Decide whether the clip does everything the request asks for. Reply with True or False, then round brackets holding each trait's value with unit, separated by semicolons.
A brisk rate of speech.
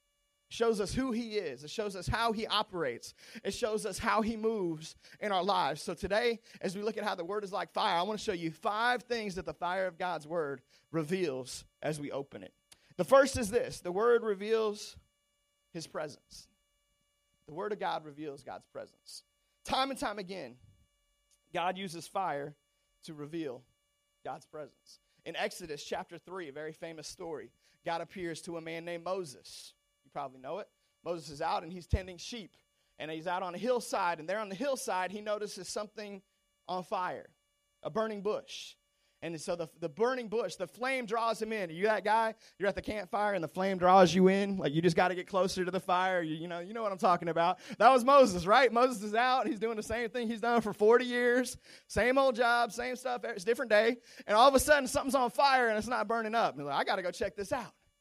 True (220 wpm)